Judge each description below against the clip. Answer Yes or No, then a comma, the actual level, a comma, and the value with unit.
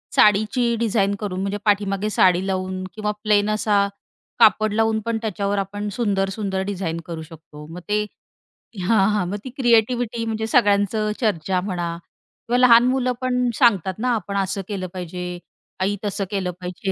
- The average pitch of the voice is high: Yes, high, 205 Hz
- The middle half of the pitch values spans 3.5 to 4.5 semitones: No, average, 2.9 semitones